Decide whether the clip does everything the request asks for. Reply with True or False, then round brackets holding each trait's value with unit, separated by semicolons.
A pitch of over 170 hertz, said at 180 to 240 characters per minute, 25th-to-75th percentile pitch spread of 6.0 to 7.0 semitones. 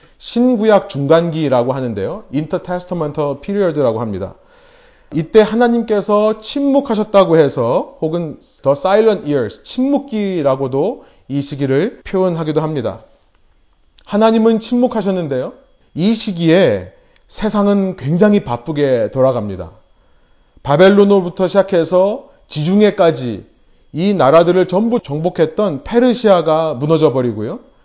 False (185 Hz; 335 characters per minute; 6.5 semitones)